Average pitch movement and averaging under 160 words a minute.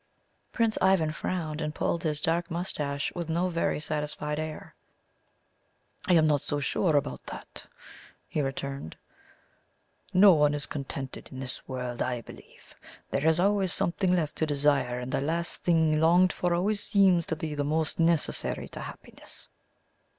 Yes: average, 3.2 semitones; average, 150 wpm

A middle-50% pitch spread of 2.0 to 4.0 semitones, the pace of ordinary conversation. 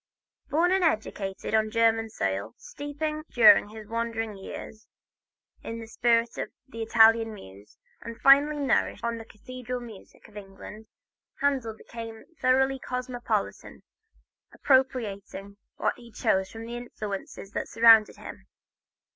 No: average, 2.9 semitones; slow, 130 wpm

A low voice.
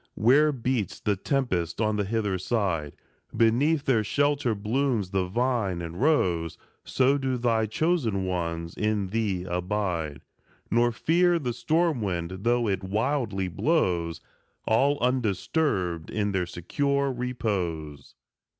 Yes: low, 110 Hz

